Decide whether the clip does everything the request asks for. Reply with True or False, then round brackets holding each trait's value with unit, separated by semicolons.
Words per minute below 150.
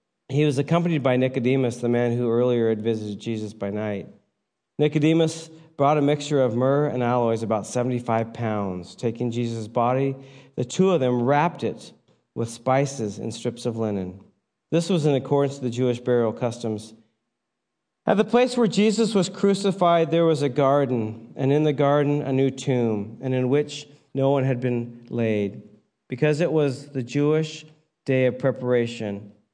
False (170 wpm)